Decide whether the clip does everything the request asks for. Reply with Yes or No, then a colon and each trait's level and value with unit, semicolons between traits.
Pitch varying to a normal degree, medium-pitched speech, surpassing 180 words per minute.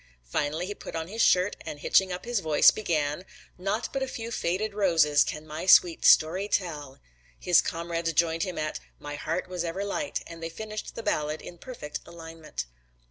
Yes: average, 4.0 semitones; medium, 170 Hz; average, 190 wpm